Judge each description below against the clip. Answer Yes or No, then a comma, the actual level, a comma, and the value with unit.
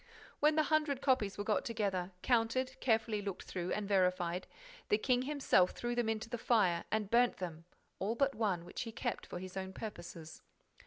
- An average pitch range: Yes, average, 4.6 semitones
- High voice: Yes, high, 215 Hz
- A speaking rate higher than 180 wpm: Yes, average, 190 wpm